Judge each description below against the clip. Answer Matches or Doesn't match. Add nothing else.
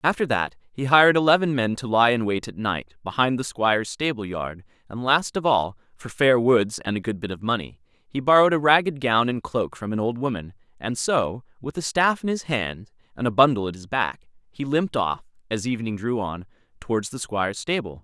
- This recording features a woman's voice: Doesn't match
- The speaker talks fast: Matches